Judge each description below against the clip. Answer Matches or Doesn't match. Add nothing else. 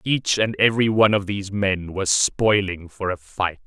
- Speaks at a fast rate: Doesn't match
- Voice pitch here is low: Matches